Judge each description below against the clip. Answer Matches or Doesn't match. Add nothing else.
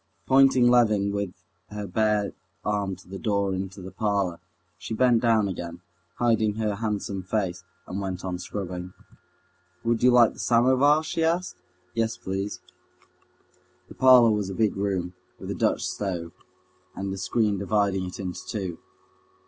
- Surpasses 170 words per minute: Doesn't match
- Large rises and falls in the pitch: Doesn't match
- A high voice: Doesn't match